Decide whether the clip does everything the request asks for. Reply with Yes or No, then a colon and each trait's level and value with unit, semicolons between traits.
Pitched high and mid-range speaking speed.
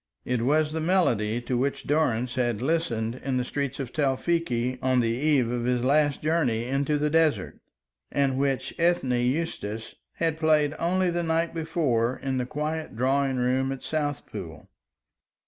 No: low, 135 Hz; average, 160 wpm